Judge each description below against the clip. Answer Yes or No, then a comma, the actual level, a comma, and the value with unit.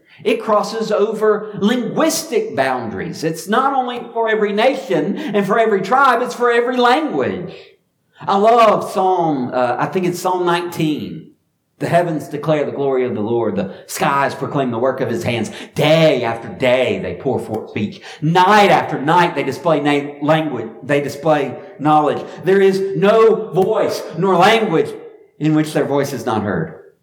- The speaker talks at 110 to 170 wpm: Yes, average, 165 wpm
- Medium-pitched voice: Yes, medium, 180 Hz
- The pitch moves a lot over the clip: Yes, wide, 6.9 semitones